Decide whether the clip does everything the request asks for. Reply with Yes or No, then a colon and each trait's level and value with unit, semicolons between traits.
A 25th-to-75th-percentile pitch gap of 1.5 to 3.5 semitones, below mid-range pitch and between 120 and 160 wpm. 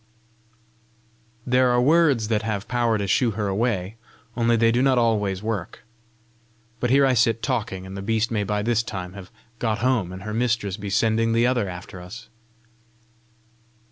No: average, 3.2 semitones; low, 110 Hz; average, 175 wpm